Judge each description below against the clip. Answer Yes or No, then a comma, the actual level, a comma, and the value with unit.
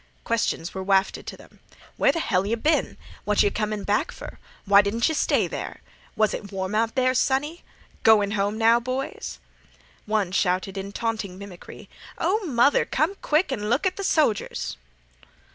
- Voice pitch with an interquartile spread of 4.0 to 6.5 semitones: Yes, average, 4.7 semitones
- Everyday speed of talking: Yes, average, 170 wpm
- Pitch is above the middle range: Yes, high, 220 Hz